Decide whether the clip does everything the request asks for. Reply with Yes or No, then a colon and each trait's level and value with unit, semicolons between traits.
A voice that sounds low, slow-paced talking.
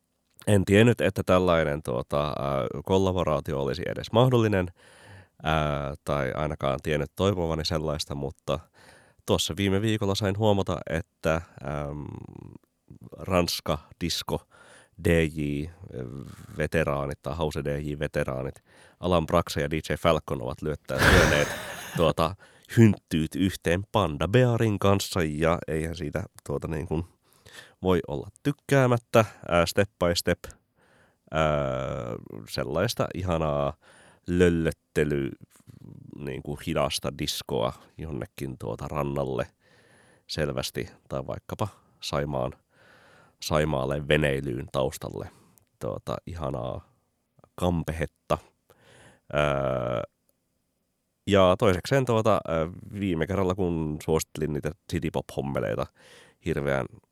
Yes: very low, 80 Hz; slow, 90 wpm